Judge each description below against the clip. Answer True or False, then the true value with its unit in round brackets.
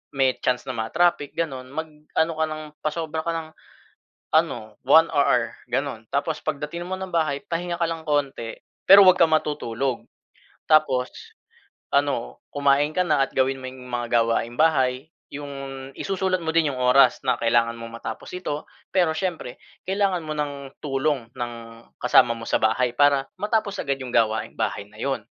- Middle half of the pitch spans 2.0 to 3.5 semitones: False (4.2 semitones)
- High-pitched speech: False (140 Hz)